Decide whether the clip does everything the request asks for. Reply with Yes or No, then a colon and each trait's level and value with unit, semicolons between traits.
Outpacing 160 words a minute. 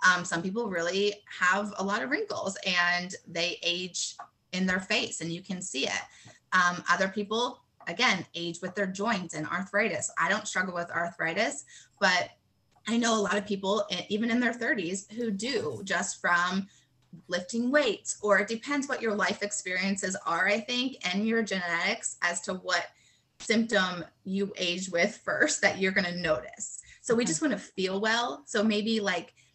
Yes: average, 180 wpm